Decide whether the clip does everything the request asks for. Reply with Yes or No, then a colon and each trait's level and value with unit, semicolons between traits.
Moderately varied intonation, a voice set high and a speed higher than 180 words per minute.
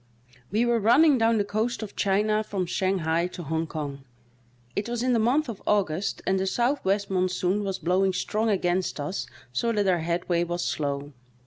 Yes: average, 3.9 semitones; high, 195 Hz; average, 190 wpm